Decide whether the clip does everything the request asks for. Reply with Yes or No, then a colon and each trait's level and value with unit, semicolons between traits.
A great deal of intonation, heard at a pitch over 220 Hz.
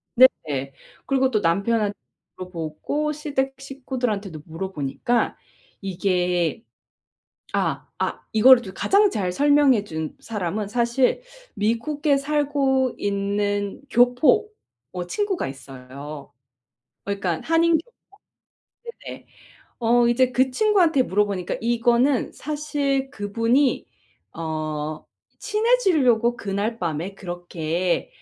Yes: wide, 6.9 semitones; high, 230 Hz